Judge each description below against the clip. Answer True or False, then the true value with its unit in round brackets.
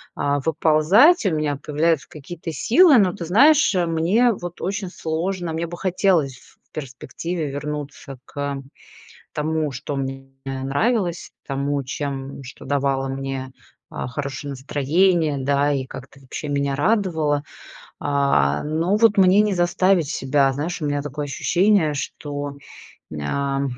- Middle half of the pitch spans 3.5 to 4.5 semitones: True (4.2 semitones)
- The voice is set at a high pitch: False (150 Hz)